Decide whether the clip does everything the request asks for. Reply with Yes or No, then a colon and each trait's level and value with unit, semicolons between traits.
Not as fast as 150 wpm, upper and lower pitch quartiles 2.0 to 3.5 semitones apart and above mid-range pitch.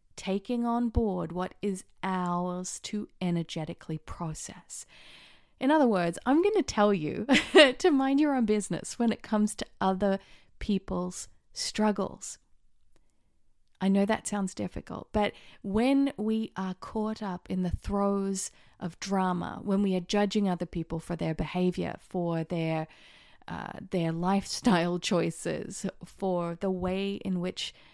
Yes: average, 140 wpm; average, 3.1 semitones; high, 195 Hz